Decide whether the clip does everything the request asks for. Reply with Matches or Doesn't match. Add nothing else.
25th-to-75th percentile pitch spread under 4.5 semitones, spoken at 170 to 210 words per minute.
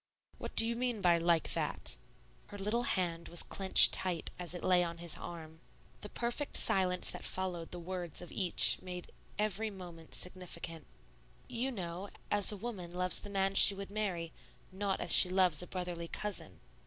Matches